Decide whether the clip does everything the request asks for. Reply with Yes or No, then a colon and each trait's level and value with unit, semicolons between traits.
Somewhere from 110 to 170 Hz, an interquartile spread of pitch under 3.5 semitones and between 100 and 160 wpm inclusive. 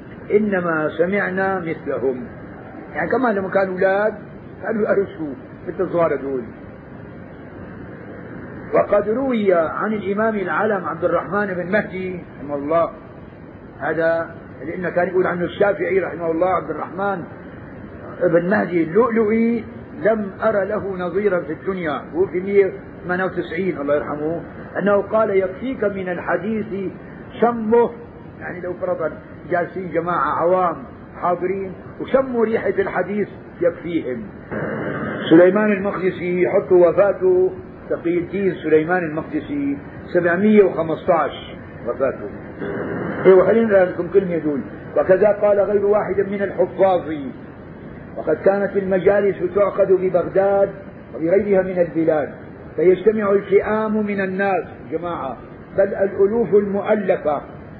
No: high, 190 Hz; average, 2.8 semitones; average, 105 wpm